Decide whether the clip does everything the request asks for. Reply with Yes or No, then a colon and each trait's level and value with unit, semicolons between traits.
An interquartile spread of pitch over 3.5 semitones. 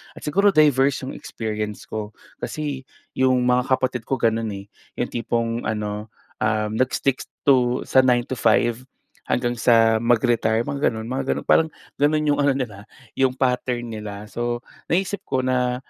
No: average, 3.0 semitones